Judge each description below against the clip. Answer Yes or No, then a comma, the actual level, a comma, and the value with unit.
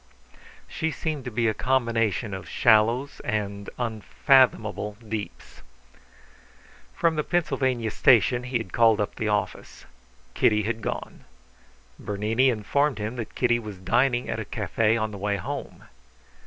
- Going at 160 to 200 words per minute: No, average, 140 wpm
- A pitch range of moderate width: Yes, average, 3.0 semitones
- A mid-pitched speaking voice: No, low, 115 Hz